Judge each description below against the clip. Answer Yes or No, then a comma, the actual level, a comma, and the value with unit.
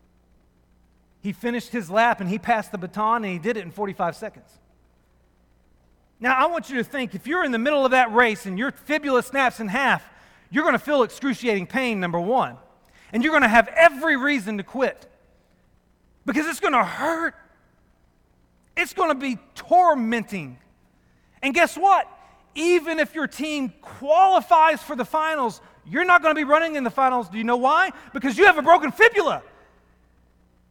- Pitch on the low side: No, high, 245 Hz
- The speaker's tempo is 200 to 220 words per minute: No, average, 170 wpm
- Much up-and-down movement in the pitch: Yes, wide, 8.0 semitones